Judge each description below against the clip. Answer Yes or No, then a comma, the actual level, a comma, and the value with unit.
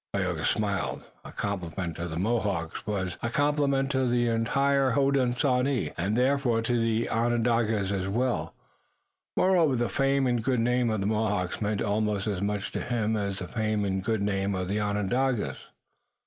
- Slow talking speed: No, average, 165 wpm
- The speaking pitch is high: No, low, 110 Hz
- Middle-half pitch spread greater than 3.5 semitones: Yes, average, 3.9 semitones